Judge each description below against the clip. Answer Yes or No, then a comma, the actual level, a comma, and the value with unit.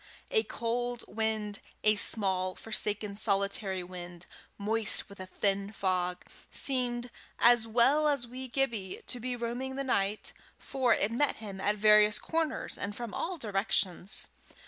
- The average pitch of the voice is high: Yes, high, 215 Hz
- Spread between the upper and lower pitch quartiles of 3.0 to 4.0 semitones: Yes, average, 3.6 semitones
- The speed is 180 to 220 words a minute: No, average, 145 wpm